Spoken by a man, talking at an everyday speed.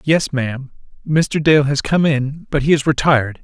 Yes: male; average, 190 wpm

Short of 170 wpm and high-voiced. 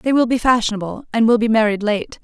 No: fast, 240 wpm; high, 225 Hz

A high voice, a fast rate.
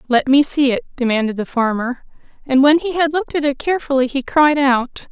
Yes: very high, 275 Hz; fast, 210 wpm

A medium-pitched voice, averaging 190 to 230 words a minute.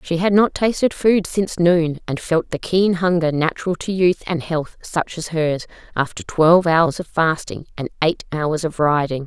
Yes: medium, 165 Hz; average, 195 wpm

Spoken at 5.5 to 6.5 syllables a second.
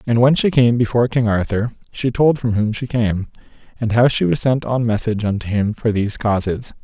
Yes: 5.6 syllables/s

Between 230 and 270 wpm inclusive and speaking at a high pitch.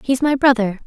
No: fast, 210 wpm; very high, 250 Hz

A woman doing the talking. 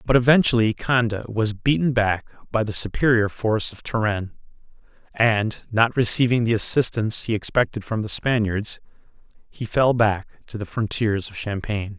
No: male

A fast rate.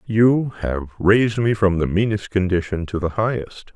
No: average, 175 wpm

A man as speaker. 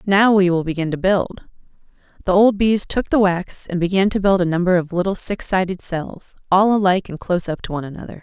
No: female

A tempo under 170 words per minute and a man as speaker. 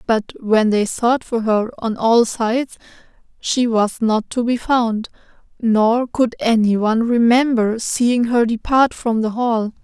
No: average, 155 wpm; female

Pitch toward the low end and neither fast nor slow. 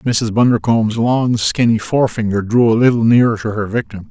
Yes: low, 115 Hz; average, 175 wpm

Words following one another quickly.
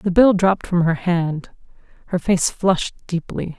No: average, 170 wpm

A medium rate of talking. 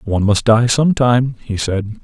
Yes: average, 175 wpm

